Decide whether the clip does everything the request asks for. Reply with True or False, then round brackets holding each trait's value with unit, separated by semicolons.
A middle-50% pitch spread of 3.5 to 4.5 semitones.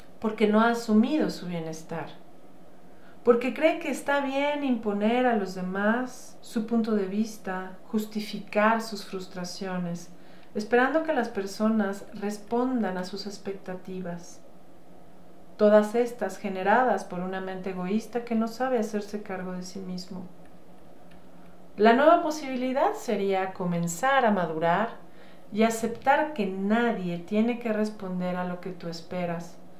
True (3.8 semitones)